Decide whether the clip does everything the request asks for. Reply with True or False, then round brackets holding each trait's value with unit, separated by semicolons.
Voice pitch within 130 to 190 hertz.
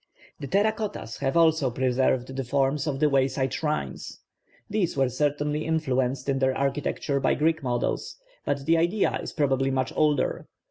True (140 Hz)